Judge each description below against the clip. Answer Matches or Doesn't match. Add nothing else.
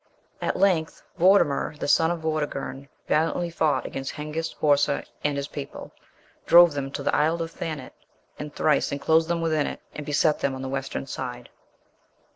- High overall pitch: Doesn't match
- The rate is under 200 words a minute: Matches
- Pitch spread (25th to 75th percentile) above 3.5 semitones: Doesn't match